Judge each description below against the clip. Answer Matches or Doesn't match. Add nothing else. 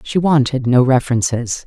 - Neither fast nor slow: Matches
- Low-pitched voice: Matches